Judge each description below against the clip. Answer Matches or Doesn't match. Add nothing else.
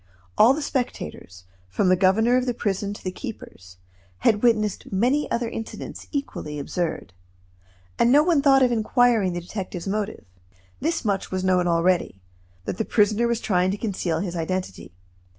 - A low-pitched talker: Doesn't match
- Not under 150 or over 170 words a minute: Matches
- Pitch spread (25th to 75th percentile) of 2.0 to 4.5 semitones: Doesn't match